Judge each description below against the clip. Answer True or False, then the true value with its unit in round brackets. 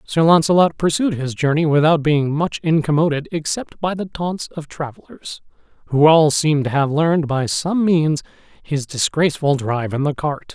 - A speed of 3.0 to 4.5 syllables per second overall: False (5.0 syllables/s)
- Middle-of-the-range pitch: True (155 Hz)